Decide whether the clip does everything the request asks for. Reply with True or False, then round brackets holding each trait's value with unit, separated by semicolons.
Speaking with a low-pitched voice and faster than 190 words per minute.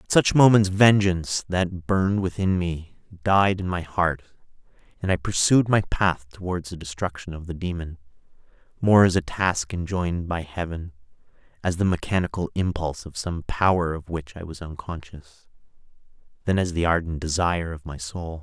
False (90 Hz; 165 wpm)